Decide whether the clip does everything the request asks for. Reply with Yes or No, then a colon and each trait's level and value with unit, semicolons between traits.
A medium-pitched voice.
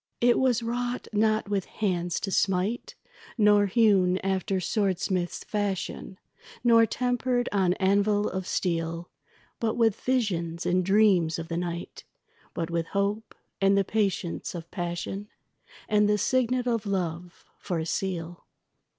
No: high, 195 Hz